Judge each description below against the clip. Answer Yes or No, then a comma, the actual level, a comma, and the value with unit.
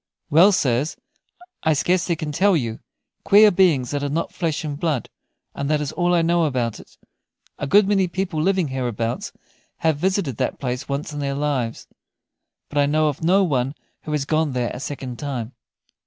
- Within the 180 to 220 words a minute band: Yes, average, 185 wpm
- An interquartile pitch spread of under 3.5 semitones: No, average, 4.3 semitones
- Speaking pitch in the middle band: Yes, medium, 150 Hz